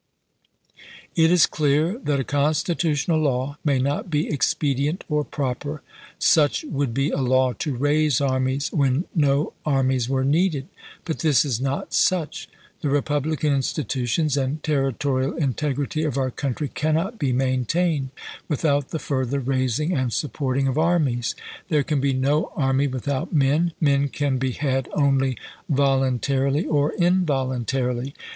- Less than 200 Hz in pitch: Yes, medium, 140 Hz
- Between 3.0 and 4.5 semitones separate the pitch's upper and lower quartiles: No, narrow, 2.5 semitones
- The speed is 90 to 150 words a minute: Yes, average, 145 wpm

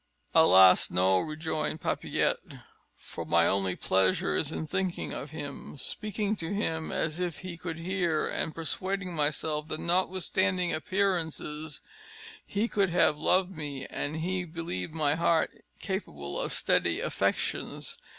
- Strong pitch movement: No, average, 3.7 semitones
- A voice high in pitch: No, medium, 160 Hz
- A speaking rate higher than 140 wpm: No, slow, 135 wpm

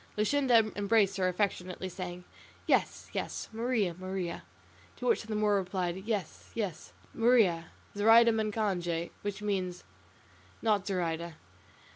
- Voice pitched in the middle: No, high, 200 Hz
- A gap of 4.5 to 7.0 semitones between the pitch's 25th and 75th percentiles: No, average, 3.3 semitones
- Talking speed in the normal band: No, slow, 115 wpm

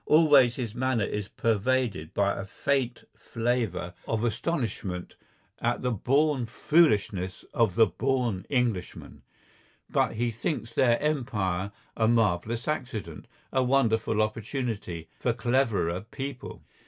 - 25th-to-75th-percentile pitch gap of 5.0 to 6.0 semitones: No, average, 4.1 semitones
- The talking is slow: Yes, slow, 115 wpm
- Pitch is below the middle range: Yes, low, 115 Hz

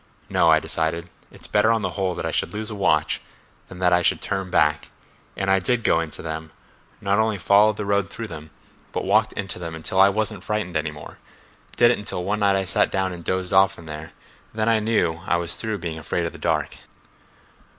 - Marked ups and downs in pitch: No, average, 3.9 semitones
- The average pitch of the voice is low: Yes, very low, 95 Hz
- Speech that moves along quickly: Yes, fast, 215 wpm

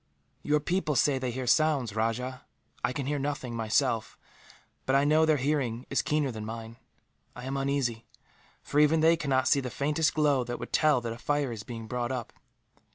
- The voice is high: No, low, 130 Hz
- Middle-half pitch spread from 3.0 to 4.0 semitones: Yes, average, 3.6 semitones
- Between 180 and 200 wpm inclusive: Yes, average, 195 wpm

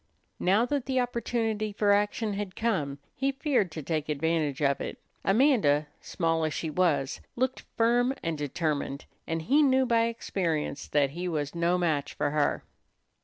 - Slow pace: No, average, 165 wpm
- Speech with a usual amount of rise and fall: No, wide, 7.3 semitones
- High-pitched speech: No, medium, 180 Hz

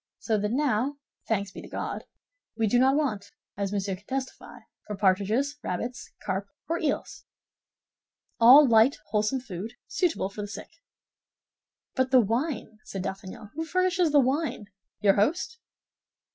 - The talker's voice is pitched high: Yes, high, 230 Hz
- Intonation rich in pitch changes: Yes, wide, 5.7 semitones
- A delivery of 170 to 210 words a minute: No, average, 145 wpm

